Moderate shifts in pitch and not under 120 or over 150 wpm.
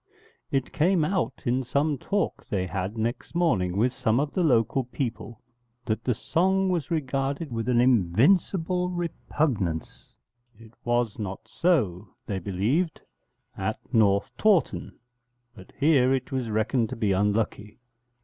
No: wide, 6.7 semitones; average, 140 wpm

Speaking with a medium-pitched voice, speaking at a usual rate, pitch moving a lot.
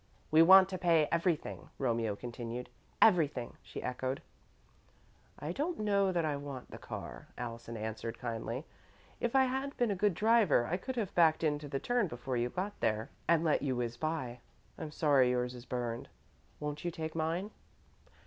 Yes: medium, 150 Hz; average, 175 wpm; wide, 6.9 semitones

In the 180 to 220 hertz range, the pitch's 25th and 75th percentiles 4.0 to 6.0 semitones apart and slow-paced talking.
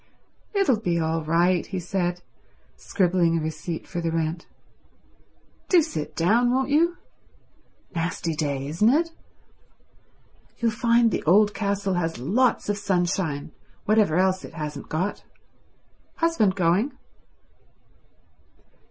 Yes: medium, 185 Hz; average, 5.0 semitones; slow, 115 wpm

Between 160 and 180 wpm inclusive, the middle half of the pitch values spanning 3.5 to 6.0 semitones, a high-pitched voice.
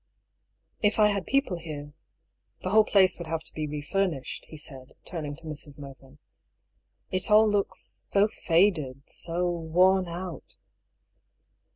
No: average, 165 wpm; average, 4.6 semitones; medium, 170 Hz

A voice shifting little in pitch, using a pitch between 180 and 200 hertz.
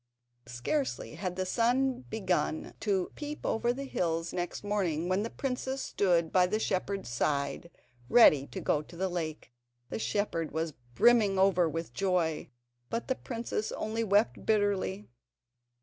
No: average, 5.2 semitones; high, 190 Hz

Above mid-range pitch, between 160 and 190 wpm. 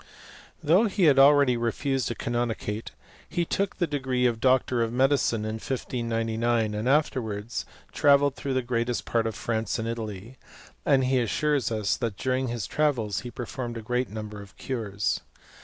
No: low, 120 Hz; average, 170 wpm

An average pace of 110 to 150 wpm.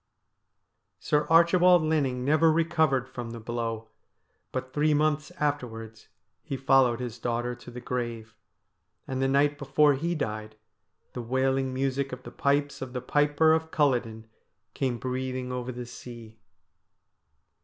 Yes: average, 140 wpm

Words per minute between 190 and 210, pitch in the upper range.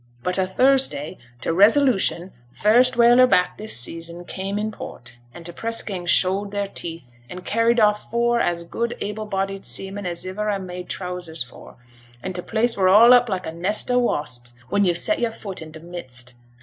Yes: average, 195 wpm; high, 195 Hz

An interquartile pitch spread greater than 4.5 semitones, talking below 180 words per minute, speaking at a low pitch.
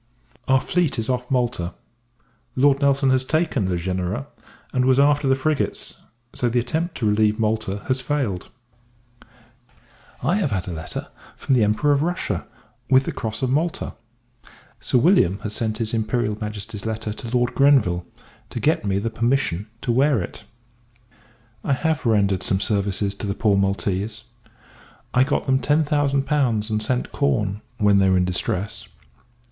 Yes: average, 5.0 semitones; average, 165 wpm; low, 115 Hz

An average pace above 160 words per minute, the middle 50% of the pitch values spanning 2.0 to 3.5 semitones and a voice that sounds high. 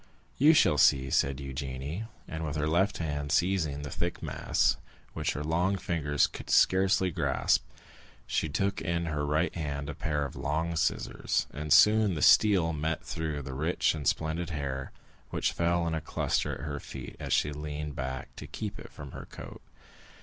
No: average, 180 wpm; average, 2.9 semitones; very low, 75 Hz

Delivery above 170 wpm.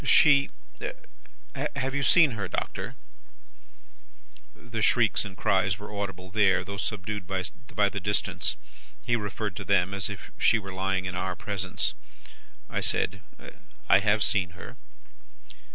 No: average, 140 wpm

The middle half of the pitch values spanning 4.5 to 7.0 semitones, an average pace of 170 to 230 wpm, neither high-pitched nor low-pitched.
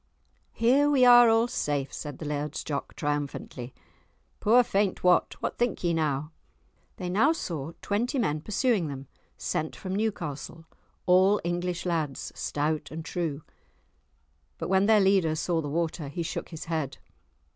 No: wide, 5.5 semitones; average, 150 wpm; medium, 170 Hz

